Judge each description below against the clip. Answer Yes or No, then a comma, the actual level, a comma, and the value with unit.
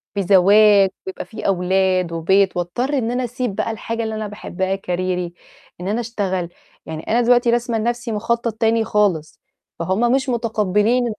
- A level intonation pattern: No, average, 3.9 semitones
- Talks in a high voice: Yes, high, 210 Hz